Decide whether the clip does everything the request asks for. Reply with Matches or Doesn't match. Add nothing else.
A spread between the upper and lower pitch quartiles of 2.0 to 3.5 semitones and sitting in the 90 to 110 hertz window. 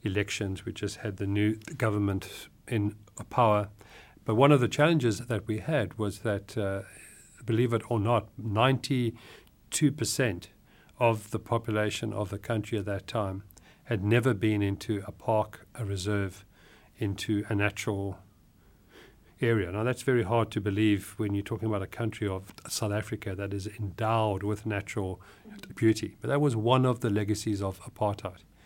Matches